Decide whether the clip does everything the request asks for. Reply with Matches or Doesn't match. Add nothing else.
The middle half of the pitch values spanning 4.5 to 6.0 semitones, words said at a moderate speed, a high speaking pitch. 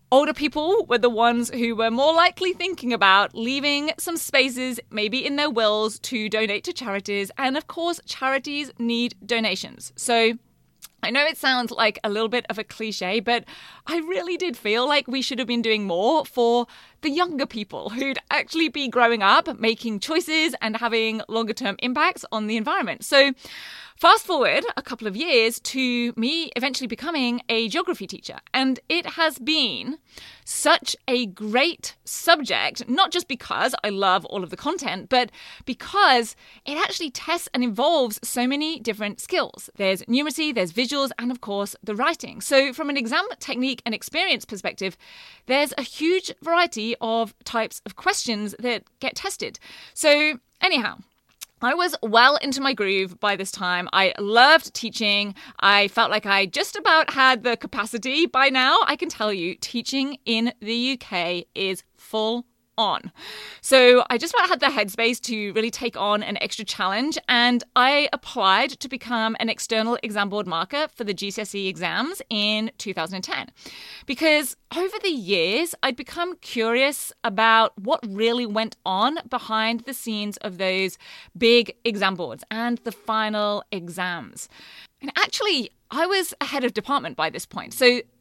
Matches